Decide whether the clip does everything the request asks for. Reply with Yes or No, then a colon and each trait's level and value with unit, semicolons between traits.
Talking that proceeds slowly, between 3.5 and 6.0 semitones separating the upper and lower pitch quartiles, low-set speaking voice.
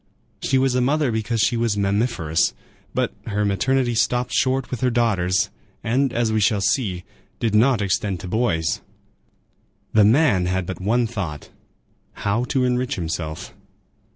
No: average, 150 wpm; average, 4.6 semitones; low, 110 Hz